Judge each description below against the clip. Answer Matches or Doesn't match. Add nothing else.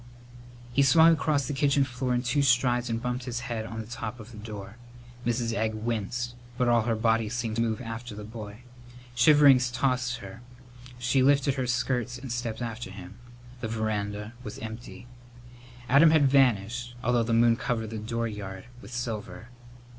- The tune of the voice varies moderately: Doesn't match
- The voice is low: Matches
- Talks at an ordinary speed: Matches